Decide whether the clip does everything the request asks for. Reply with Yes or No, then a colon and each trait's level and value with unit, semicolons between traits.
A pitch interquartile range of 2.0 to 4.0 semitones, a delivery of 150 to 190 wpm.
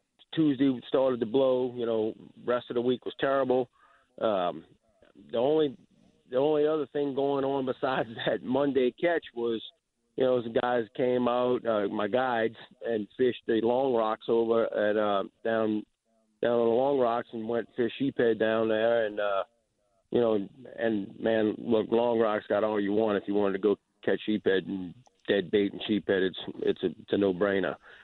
Yes: average, 3.0 semitones; average, 185 wpm